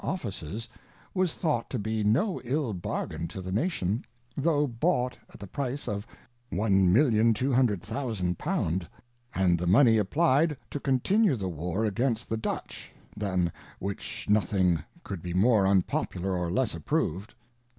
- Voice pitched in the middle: No, low, 110 Hz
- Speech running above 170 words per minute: No, slow, 135 wpm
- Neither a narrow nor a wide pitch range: No, wide, 6.0 semitones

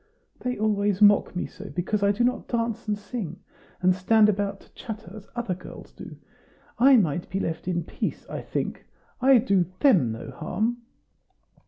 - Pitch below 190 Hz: No, high, 205 Hz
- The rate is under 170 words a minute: No, average, 175 wpm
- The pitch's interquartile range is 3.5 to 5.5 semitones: Yes, average, 3.8 semitones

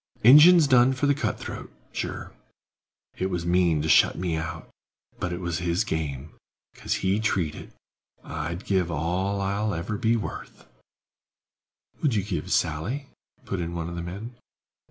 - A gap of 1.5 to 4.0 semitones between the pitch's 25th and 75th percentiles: No, average, 4.6 semitones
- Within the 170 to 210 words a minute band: No, average, 160 wpm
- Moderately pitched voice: No, very low, 90 Hz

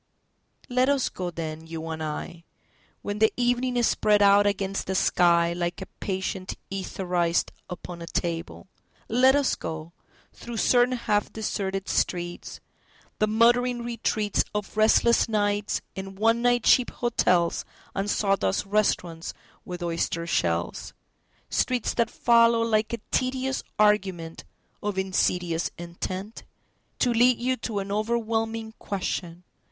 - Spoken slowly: Yes, slow, 115 wpm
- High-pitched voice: Yes, high, 205 Hz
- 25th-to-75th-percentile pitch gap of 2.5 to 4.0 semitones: No, average, 4.8 semitones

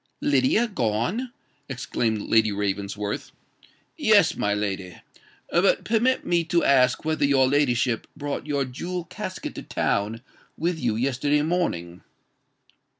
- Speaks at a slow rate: Yes, slow, 115 wpm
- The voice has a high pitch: No, low, 135 Hz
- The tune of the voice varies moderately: No, wide, 7.7 semitones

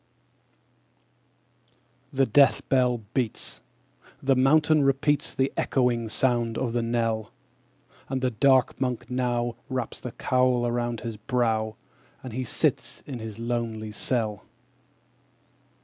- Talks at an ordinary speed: No, slow, 120 wpm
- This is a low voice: Yes, low, 120 Hz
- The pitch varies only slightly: Yes, narrow, 2.2 semitones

